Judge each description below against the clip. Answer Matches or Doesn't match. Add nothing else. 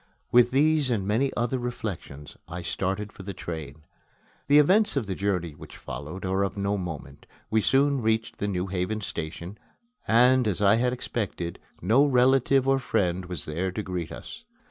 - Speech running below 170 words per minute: Doesn't match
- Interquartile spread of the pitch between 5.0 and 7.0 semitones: Matches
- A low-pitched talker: Matches